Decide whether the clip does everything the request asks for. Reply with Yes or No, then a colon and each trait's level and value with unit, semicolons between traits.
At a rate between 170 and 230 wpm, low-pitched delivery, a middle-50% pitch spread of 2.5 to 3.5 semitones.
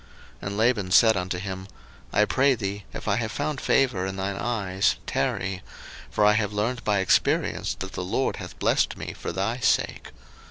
Yes: average, 190 wpm; low, 105 Hz; average, 3.0 semitones